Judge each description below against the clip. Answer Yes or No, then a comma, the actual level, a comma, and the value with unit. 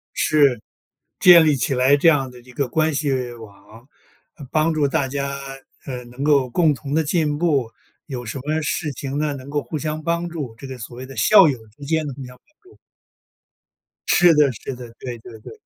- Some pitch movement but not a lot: Yes, average, 3.5 semitones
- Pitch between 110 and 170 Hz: Yes, medium, 140 Hz